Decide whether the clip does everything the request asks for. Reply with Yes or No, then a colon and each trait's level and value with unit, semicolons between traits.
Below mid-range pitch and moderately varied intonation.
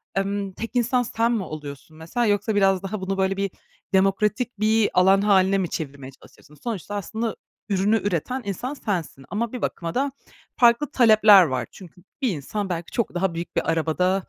No: high, 195 Hz; average, 3.8 semitones